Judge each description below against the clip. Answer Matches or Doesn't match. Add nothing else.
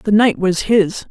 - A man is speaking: Doesn't match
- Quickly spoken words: Matches